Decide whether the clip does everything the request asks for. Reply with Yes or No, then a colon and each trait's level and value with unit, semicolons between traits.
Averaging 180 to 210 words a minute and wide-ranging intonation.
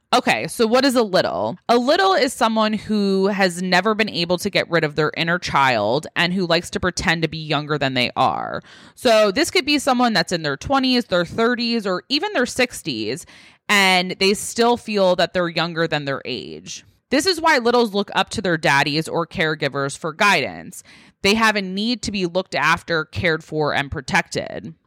Yes: average, 200 wpm; wide, 5.9 semitones